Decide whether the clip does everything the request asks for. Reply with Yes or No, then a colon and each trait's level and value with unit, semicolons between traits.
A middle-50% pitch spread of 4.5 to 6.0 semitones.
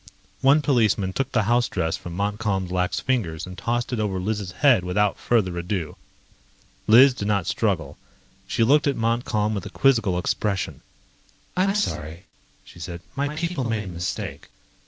Yes: average, 5.2 semitones